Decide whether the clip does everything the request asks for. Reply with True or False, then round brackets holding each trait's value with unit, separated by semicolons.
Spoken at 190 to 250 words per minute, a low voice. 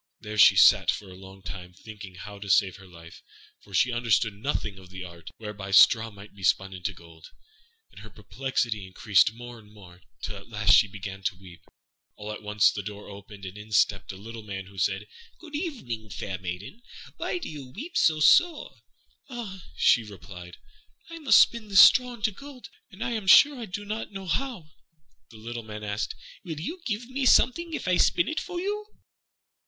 True (200 wpm; 105 Hz)